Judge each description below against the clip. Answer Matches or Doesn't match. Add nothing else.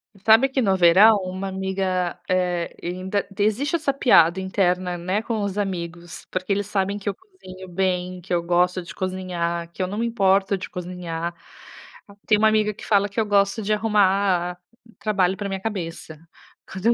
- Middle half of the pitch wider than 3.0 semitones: Doesn't match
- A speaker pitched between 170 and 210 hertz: Matches